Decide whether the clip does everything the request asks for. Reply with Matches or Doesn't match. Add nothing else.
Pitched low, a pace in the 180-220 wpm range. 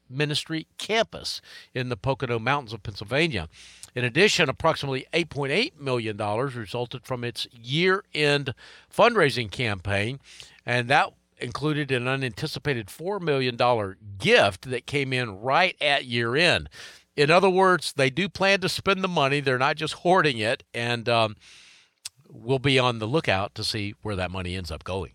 Doesn't match